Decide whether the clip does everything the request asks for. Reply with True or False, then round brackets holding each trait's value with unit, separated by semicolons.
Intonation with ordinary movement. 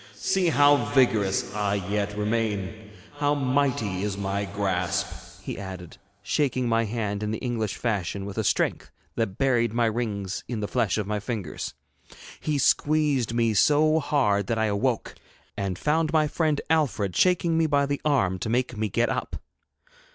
False (5.8 semitones)